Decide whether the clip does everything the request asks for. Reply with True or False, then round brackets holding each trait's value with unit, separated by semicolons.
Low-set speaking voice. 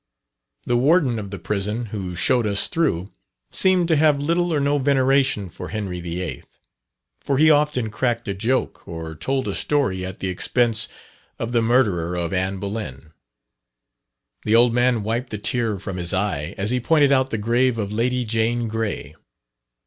True (115 Hz)